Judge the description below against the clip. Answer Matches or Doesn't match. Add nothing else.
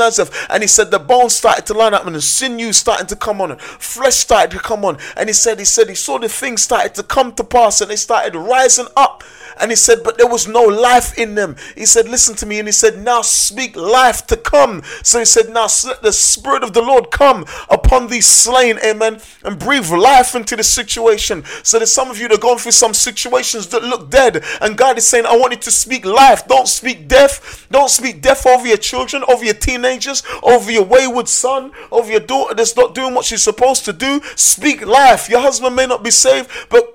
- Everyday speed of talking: Doesn't match